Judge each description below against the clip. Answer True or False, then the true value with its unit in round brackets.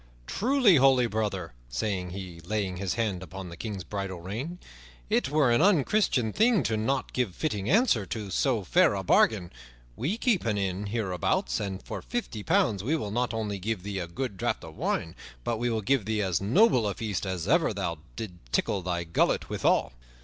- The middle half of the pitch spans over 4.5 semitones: True (5.2 semitones)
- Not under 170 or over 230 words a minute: True (190 wpm)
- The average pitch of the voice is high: False (105 Hz)